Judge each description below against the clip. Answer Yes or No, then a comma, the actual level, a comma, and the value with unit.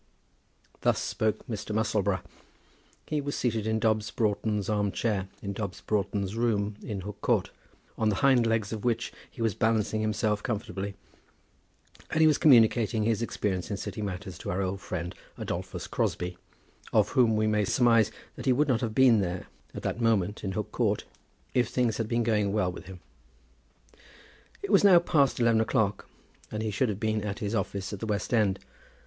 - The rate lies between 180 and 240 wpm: Yes, average, 185 wpm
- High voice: No, low, 110 Hz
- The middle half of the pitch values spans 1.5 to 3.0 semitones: Yes, narrow, 2.4 semitones